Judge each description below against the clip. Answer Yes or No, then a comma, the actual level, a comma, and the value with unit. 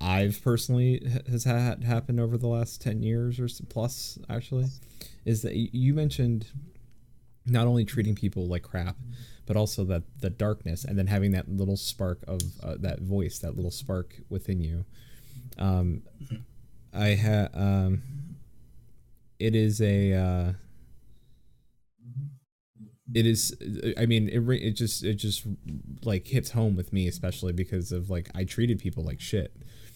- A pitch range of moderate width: Yes, average, 4.0 semitones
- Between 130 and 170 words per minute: Yes, average, 150 wpm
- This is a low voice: Yes, low, 110 Hz